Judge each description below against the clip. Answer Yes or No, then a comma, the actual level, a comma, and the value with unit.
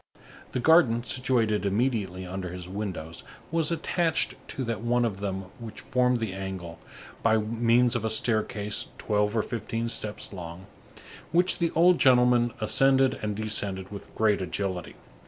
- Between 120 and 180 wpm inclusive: Yes, average, 150 wpm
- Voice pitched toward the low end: Yes, low, 110 Hz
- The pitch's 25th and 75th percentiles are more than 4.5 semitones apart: No, average, 4.0 semitones